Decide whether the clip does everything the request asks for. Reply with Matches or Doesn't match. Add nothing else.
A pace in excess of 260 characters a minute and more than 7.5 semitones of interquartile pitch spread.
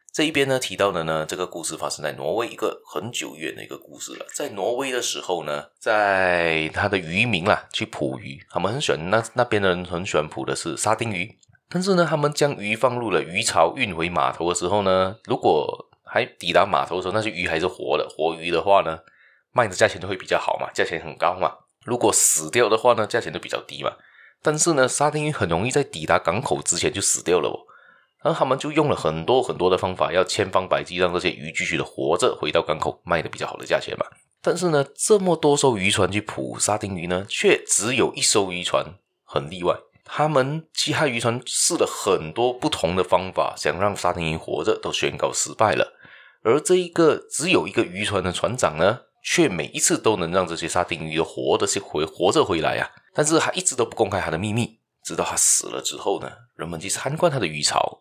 Matches